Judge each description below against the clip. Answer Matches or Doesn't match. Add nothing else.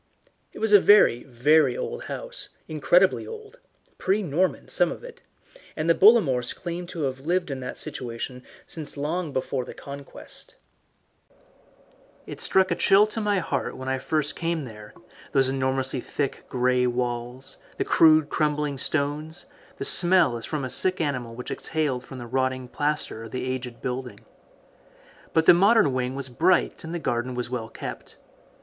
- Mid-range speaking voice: Matches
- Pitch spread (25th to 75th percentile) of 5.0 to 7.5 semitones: Matches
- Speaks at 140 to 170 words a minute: Matches